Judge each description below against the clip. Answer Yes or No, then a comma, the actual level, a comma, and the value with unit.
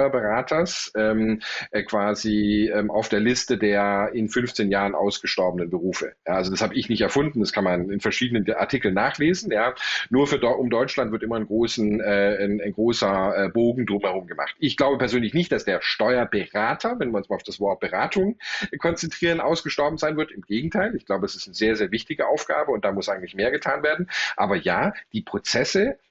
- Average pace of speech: No, fast, 195 wpm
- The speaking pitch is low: Yes, low, 110 Hz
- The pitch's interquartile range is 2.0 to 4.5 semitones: No, average, 4.9 semitones